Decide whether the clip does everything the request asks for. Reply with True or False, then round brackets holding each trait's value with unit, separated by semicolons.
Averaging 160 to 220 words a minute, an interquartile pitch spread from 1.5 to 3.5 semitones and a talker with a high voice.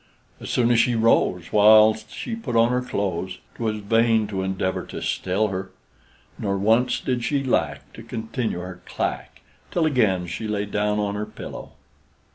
False (170 wpm; 3.2 semitones; 110 Hz)